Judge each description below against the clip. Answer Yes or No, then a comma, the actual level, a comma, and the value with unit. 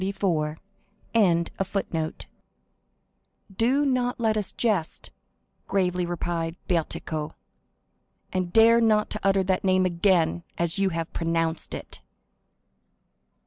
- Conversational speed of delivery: No, slow, 100 wpm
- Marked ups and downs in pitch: No, average, 4.1 semitones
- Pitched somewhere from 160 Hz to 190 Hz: Yes, medium, 185 Hz